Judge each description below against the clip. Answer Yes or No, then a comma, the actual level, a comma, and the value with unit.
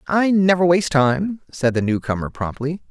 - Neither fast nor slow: Yes, average, 165 wpm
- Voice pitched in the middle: Yes, medium, 155 Hz